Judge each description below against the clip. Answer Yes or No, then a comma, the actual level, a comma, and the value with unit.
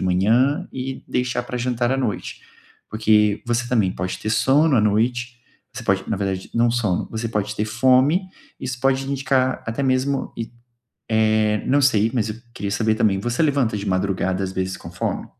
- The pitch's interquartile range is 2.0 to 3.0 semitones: No, average, 3.7 semitones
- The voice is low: Yes, low, 115 Hz